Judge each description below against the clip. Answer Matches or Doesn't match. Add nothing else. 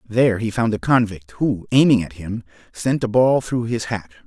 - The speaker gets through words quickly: Matches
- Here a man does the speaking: Matches